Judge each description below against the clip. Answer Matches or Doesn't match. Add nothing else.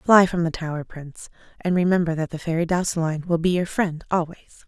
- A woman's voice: Matches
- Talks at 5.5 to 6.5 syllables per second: Matches